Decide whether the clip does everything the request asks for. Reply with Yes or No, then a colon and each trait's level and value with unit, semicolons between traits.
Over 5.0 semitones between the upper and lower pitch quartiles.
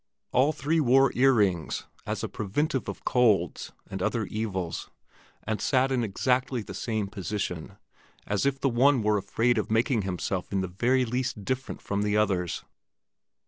No: average, 4.6 semitones